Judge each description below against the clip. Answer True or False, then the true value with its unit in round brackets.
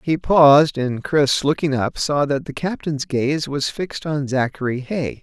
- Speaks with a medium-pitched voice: True (145 Hz)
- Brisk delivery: False (185 wpm)